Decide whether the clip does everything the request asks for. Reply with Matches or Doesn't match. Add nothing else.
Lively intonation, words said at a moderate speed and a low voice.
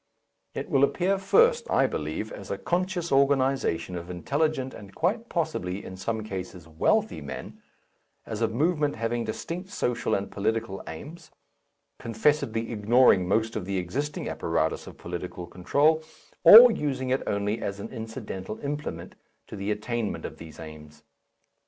Matches